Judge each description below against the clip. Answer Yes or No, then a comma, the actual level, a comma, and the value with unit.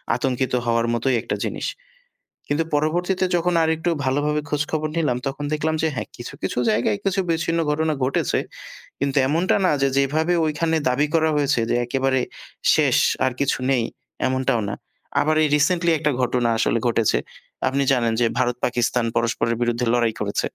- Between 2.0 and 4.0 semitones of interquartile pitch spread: No, average, 4.4 semitones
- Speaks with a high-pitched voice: No, medium, 140 Hz